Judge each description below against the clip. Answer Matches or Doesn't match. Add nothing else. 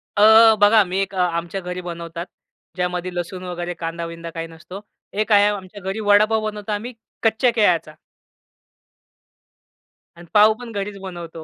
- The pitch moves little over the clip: Doesn't match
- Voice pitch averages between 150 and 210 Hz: Matches